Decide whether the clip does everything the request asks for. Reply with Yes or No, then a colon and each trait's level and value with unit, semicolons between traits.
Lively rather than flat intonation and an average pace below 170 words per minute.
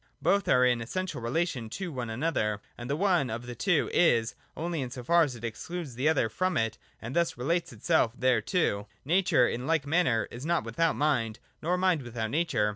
No: wide, 6.3 semitones; average, 200 wpm